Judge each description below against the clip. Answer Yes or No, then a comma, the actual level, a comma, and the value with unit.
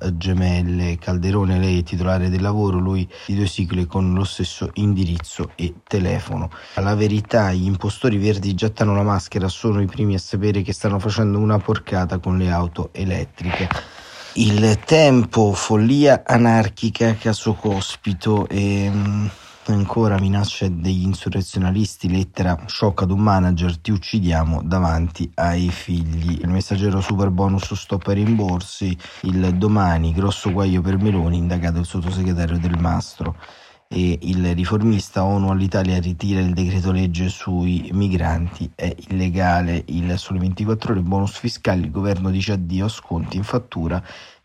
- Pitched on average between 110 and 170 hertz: No, very low, 95 Hz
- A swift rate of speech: No, average, 145 wpm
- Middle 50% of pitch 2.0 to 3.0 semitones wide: Yes, narrow, 2.4 semitones